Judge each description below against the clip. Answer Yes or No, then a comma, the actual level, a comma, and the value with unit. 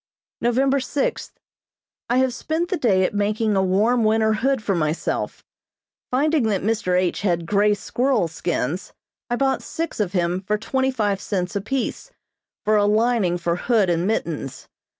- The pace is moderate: Yes, average, 160 wpm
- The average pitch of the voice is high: Yes, high, 210 Hz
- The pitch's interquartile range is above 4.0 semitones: Yes, average, 5.0 semitones